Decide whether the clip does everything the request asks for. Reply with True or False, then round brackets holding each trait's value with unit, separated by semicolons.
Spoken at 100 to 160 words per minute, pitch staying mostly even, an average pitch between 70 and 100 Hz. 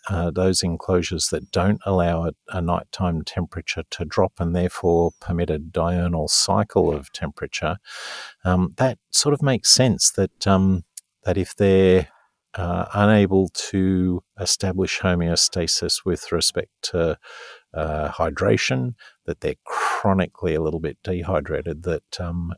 True (135 wpm; 1.9 semitones; 90 Hz)